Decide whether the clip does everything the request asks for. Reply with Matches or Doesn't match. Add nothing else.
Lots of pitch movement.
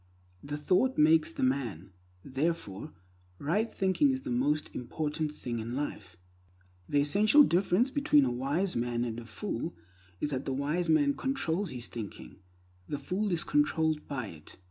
Matches